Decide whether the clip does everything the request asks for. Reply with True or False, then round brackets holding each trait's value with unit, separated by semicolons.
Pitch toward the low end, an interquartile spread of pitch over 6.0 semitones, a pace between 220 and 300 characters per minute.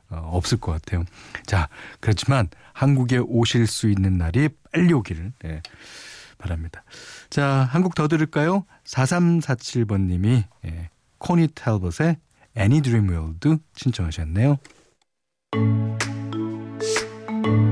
True (110 Hz; 6.4 semitones; 230 characters per minute)